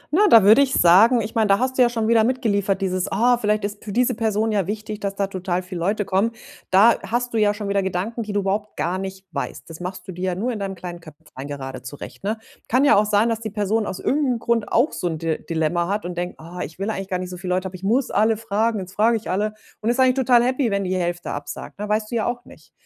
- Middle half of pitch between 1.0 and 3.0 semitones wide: No, average, 3.6 semitones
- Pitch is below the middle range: No, high, 205 Hz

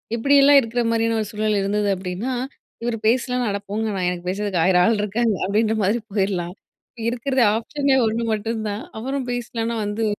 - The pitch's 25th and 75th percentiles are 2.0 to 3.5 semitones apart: Yes, average, 2.9 semitones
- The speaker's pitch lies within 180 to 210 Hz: No, high, 220 Hz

